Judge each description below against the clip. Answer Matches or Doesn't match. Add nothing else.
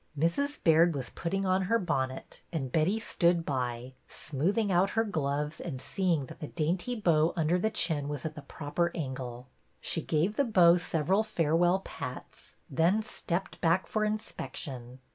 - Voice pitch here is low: Doesn't match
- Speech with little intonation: Doesn't match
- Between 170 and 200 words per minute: Doesn't match